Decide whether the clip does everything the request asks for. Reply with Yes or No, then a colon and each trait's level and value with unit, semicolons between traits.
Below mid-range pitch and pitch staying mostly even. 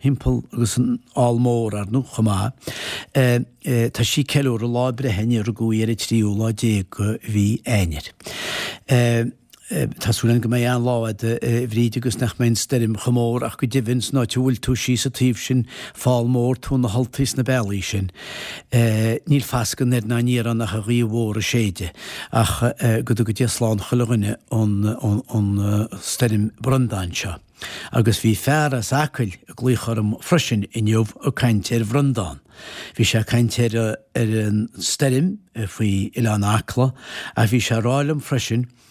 Yes: low, 115 Hz; narrow, 2.3 semitones